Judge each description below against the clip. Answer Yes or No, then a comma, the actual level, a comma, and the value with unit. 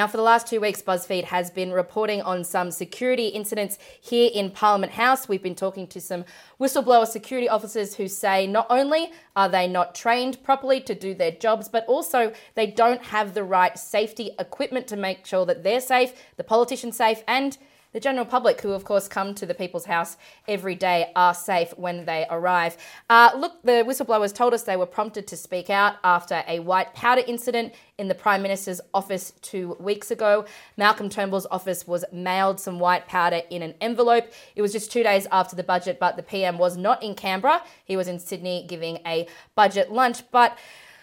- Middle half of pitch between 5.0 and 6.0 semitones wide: No, average, 4.2 semitones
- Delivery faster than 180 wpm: Yes, average, 200 wpm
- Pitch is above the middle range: Yes, high, 205 Hz